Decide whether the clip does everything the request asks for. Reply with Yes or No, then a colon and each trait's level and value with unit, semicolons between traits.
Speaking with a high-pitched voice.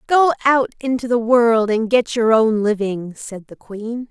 Yes: high, 230 Hz